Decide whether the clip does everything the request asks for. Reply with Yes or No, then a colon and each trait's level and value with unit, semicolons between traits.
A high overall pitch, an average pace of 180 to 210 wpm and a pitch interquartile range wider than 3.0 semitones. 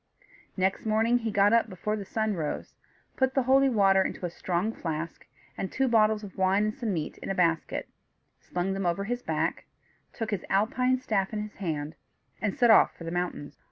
Yes: high, 200 Hz; average, 200 wpm; average, 3.8 semitones